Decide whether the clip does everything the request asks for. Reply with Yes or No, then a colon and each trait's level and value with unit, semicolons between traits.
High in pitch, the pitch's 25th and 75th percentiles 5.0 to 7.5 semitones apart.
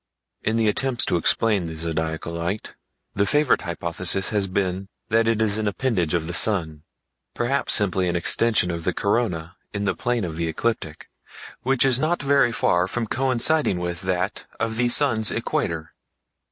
No: low, 100 Hz; wide, 5.4 semitones